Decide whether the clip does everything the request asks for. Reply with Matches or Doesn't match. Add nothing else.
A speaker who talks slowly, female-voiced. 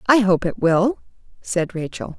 Doesn't match